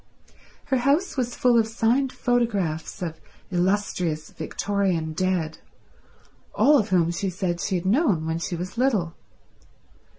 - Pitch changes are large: Yes, wide, 5.9 semitones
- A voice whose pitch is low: No, high, 190 Hz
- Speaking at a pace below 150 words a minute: Yes, slow, 135 wpm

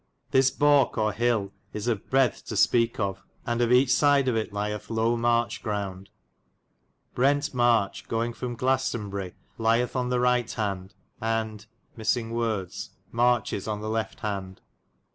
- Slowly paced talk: No, average, 145 wpm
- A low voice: Yes, low, 115 Hz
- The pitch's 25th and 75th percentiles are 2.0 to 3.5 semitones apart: Yes, average, 2.8 semitones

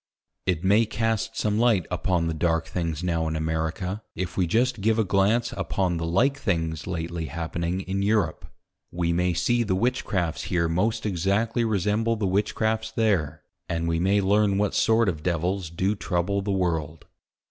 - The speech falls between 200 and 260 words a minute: No, average, 170 wpm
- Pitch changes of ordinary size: Yes, average, 4.3 semitones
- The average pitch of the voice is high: No, very low, 95 Hz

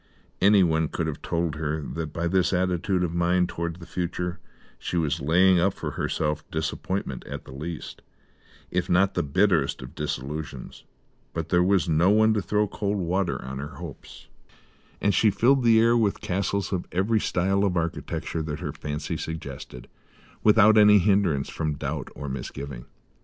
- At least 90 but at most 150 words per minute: No, average, 165 wpm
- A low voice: Yes, very low, 85 Hz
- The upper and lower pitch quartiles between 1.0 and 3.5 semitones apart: No, average, 4.1 semitones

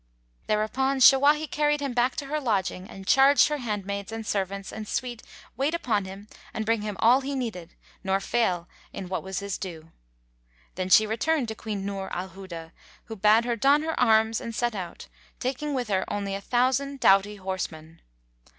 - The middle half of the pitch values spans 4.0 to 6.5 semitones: Yes, average, 5.1 semitones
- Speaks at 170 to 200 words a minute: Yes, average, 180 wpm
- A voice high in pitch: Yes, high, 215 Hz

